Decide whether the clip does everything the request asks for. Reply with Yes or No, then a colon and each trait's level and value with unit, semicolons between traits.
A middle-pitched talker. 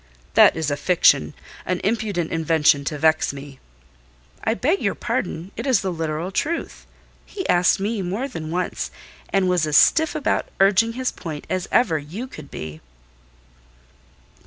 Yes: medium, 180 Hz